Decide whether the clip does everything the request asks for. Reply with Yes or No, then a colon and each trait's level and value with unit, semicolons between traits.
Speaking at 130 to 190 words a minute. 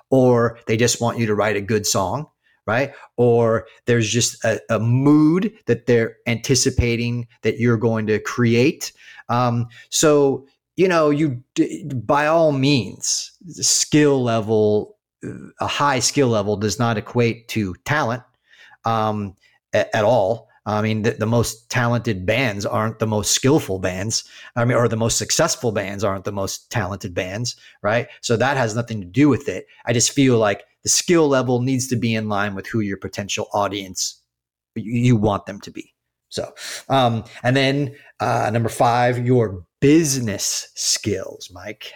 Yes: average, 165 wpm